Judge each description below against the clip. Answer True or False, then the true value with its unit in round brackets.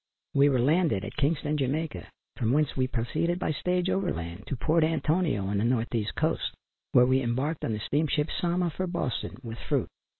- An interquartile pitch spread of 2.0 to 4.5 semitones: False (5.6 semitones)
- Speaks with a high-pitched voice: False (145 Hz)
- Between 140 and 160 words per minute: False (195 wpm)